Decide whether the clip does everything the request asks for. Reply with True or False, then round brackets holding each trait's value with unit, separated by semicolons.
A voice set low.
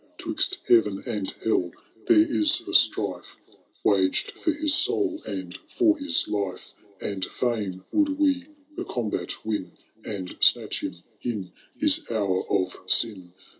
True (110 Hz)